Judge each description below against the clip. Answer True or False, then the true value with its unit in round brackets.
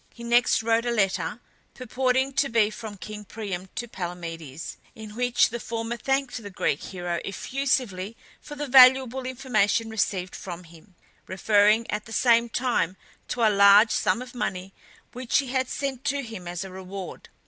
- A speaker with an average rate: True (170 wpm)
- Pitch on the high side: True (225 Hz)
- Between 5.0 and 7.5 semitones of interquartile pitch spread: False (4.5 semitones)